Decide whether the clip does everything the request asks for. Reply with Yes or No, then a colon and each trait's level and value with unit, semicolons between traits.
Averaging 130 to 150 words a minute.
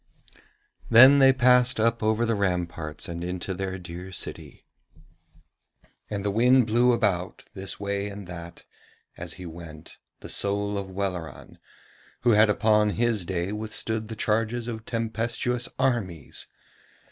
Yes: slow, 135 wpm